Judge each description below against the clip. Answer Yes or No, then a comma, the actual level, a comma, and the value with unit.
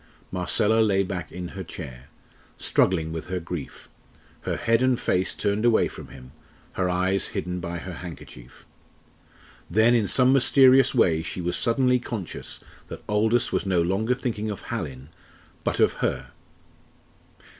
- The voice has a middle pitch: No, very low, 95 Hz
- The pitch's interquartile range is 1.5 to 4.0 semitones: No, average, 4.8 semitones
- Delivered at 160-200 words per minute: No, average, 150 wpm